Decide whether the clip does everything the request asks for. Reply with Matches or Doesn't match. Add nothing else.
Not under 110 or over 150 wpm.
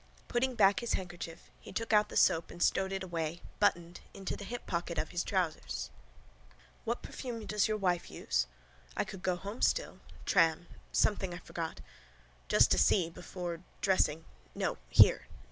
Doesn't match